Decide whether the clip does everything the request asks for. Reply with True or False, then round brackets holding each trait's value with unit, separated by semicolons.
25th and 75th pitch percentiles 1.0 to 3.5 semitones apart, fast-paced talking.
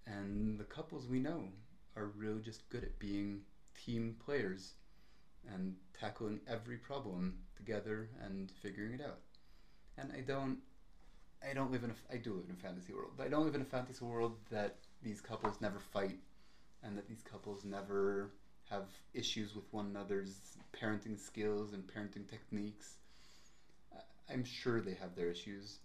True (3.0 semitones; 165 wpm)